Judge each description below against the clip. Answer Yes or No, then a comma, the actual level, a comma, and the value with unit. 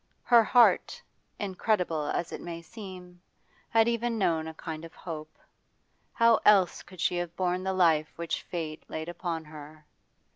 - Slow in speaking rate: No, average, 155 wpm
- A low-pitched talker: No, medium, 175 Hz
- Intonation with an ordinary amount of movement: Yes, average, 3.5 semitones